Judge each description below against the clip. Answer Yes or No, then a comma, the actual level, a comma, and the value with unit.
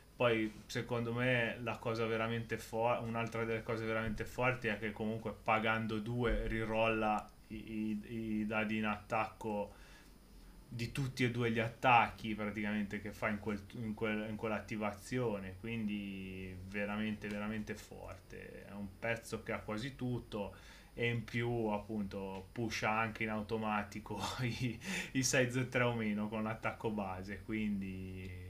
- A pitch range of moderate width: No, narrow, 1.7 semitones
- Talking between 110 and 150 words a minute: Yes, average, 140 wpm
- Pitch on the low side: Yes, low, 110 Hz